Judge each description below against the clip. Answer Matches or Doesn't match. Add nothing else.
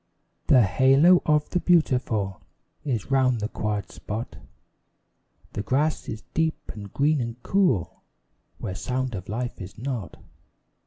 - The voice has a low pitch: Matches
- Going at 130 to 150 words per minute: Matches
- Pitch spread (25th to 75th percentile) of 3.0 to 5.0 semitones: Doesn't match